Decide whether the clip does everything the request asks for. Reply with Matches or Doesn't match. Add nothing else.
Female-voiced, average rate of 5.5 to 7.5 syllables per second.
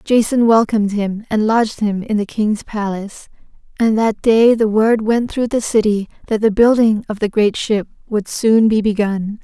Doesn't match